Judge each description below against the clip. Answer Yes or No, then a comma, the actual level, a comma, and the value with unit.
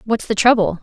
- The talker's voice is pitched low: No, high, 215 Hz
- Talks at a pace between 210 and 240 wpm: Yes, fast, 220 wpm